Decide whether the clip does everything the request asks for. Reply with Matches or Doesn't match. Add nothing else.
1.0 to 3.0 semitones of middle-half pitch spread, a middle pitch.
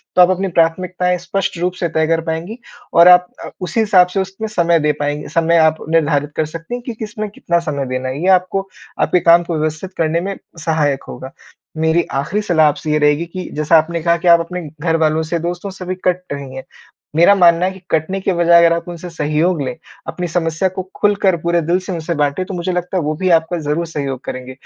Matches